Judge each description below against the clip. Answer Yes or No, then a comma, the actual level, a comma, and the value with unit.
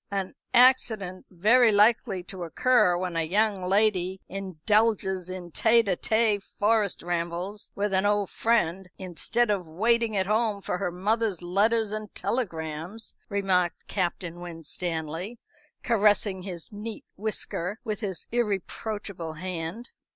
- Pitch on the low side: No, high, 195 Hz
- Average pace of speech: No, slow, 130 wpm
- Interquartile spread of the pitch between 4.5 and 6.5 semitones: No, average, 3.5 semitones